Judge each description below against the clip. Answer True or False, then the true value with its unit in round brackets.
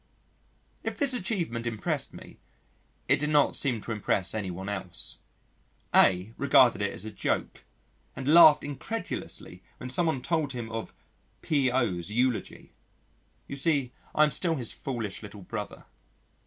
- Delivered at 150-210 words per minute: False (140 wpm)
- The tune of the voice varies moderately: False (6.0 semitones)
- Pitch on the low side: True (125 Hz)